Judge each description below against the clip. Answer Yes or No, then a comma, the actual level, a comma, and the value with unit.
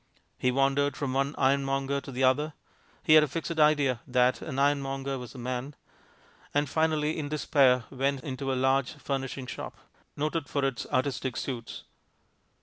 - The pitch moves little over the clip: Yes, narrow, 1.9 semitones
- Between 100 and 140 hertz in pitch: Yes, low, 135 Hz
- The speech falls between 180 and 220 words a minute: No, average, 160 wpm